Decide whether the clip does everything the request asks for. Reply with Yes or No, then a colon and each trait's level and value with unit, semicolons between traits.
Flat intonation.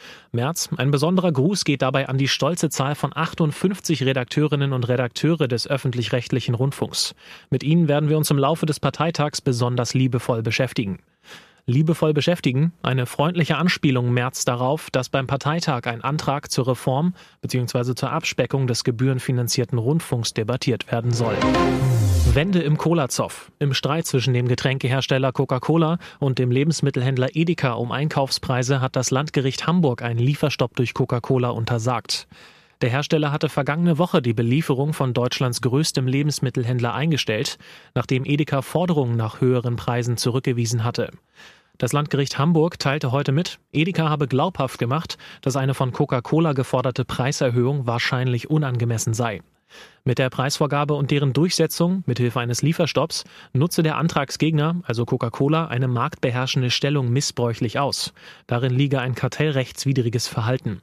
No: average, 3.2 semitones